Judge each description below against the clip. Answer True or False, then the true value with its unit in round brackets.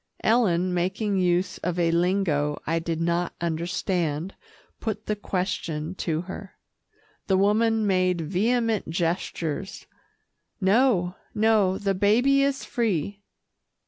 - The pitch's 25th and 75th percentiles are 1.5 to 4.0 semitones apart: True (3.6 semitones)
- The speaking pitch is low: False (185 Hz)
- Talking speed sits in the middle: False (110 wpm)